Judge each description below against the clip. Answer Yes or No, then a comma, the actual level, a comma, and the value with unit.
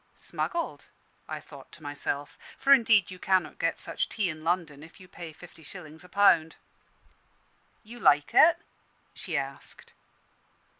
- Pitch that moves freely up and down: No, average, 4.6 semitones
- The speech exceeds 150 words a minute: No, average, 145 wpm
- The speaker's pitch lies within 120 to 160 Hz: No, medium, 170 Hz